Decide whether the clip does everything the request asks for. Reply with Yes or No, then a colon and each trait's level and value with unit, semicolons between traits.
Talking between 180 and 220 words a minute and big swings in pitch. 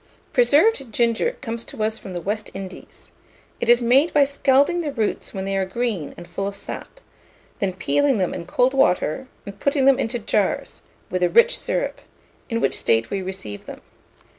Yes: average, 190 wpm; wide, 6.0 semitones